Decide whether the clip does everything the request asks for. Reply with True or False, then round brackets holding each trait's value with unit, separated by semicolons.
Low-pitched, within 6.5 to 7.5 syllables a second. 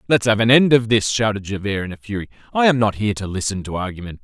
True (110 Hz; 6.8 syllables/s)